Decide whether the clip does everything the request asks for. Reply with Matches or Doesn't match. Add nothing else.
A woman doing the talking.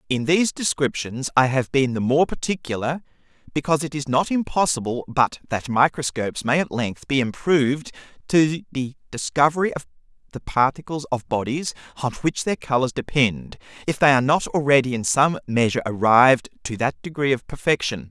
Doesn't match